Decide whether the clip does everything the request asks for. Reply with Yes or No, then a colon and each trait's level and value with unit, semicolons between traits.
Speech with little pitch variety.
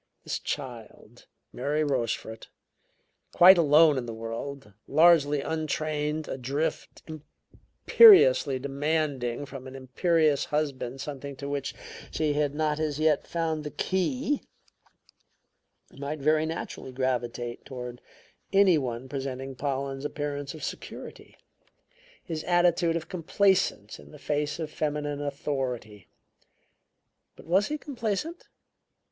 No: average, 3.1 semitones